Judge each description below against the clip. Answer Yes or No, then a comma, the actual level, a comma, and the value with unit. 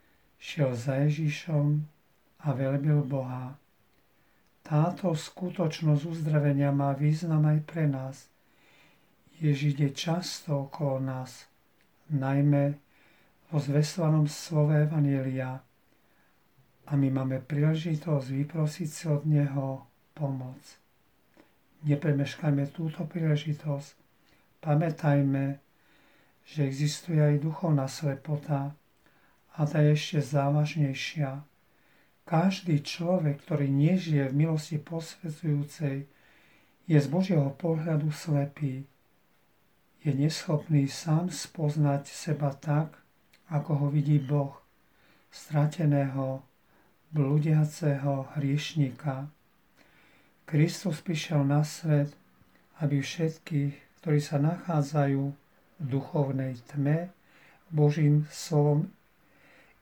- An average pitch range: No, narrow, 1.8 semitones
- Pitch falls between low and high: Yes, medium, 150 Hz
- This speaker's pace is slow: Yes, slow, 85 wpm